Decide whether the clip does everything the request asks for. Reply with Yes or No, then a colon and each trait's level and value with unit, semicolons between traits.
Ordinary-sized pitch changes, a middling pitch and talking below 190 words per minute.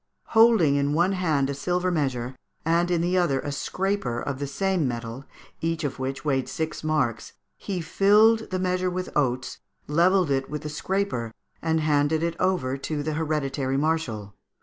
Yes: average, 4.9 semitones; medium, 155 Hz; average, 170 wpm